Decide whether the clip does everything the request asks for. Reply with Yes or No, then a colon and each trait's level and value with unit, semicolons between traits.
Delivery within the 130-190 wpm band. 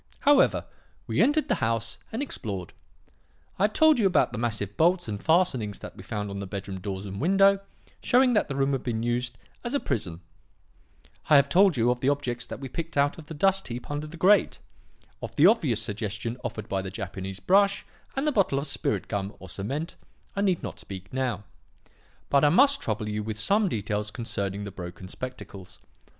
No: average, 200 wpm